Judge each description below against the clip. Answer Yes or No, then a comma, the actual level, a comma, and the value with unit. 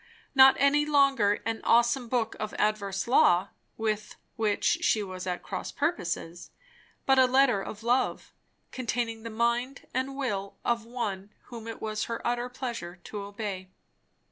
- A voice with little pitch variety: No, average, 3.7 semitones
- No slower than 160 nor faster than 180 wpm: No, average, 150 wpm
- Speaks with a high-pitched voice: Yes, high, 230 Hz